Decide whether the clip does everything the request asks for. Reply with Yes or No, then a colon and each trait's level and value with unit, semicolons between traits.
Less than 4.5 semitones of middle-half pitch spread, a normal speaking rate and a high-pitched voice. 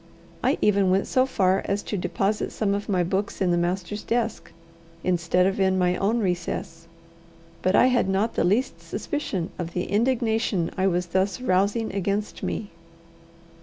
Yes: average, 2.7 semitones; average, 165 wpm; high, 195 Hz